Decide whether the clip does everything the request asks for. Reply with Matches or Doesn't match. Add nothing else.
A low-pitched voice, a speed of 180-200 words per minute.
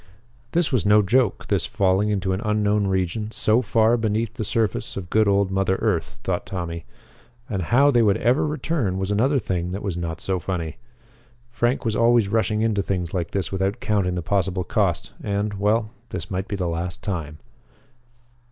Matches